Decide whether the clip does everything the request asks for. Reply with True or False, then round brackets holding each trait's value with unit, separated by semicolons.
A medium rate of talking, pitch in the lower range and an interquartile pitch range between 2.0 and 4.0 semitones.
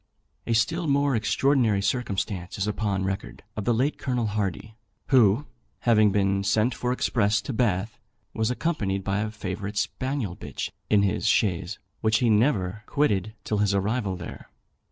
True (155 wpm; 105 Hz; 3.7 semitones)